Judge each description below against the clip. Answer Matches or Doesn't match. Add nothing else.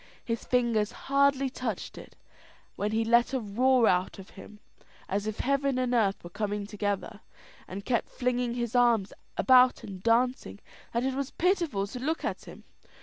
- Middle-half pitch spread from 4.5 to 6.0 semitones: Doesn't match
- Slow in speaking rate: Doesn't match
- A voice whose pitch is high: Matches